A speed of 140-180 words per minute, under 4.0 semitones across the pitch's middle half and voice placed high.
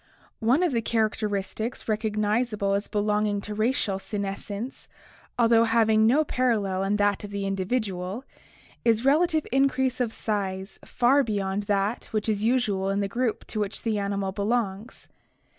Yes: average, 160 wpm; average, 2.9 semitones; high, 215 Hz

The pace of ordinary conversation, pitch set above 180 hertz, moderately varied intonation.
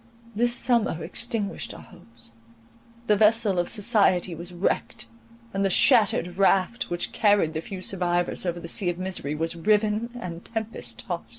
Yes: average, 160 wpm; high, 190 Hz; average, 3.6 semitones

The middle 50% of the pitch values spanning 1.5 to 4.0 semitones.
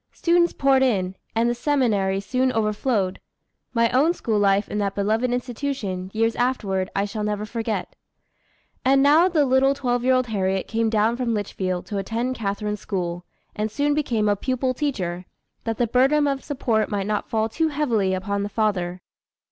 No: average, 4.4 semitones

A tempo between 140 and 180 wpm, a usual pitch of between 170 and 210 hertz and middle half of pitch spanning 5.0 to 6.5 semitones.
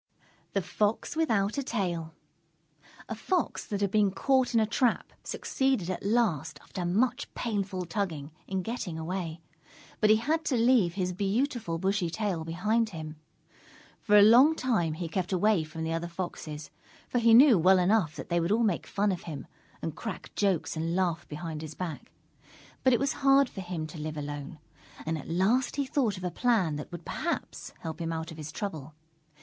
No: average, 190 wpm; high, 190 Hz; wide, 5.5 semitones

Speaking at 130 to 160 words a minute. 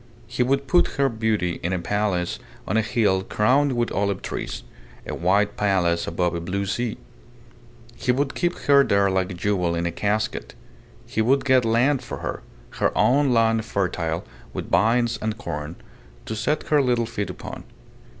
No: average, 175 wpm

